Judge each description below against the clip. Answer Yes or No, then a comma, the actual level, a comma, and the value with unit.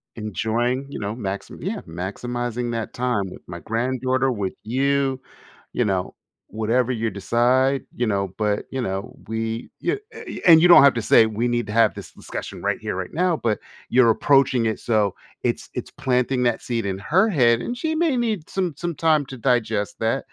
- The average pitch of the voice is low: Yes, low, 120 Hz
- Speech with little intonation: No, average, 3.7 semitones